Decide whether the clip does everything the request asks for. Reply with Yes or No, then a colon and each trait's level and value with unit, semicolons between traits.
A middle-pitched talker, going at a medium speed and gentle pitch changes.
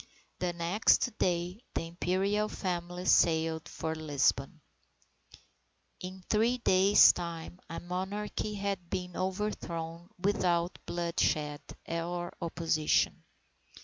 No: medium, 175 Hz; slow, 95 wpm; narrow, 2.2 semitones